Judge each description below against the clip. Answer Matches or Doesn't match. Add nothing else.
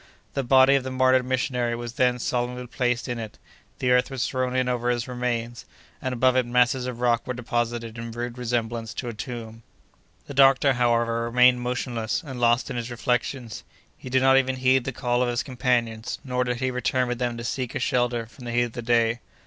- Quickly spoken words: Matches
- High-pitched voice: Doesn't match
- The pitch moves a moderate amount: Doesn't match